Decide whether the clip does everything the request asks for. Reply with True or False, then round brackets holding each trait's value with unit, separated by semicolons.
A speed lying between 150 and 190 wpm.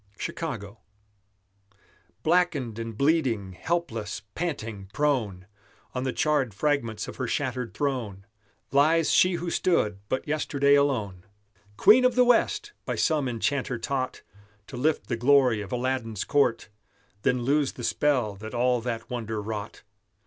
False (135 wpm)